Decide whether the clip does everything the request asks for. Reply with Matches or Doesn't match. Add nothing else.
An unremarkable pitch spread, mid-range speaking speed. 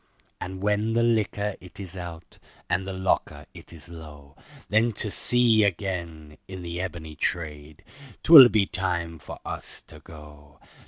Matches